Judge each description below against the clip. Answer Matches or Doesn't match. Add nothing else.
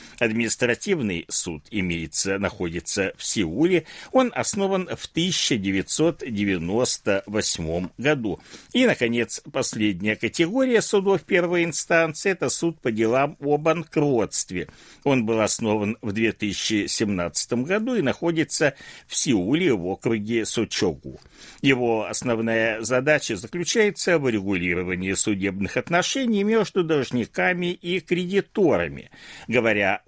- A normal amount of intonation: Doesn't match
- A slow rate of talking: Matches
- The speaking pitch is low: Matches